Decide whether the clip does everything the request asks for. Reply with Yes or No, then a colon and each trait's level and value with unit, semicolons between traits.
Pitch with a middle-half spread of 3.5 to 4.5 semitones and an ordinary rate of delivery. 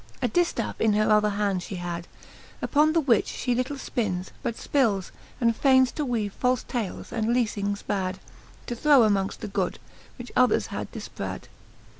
Yes: average, 3.9 semitones; average, 170 wpm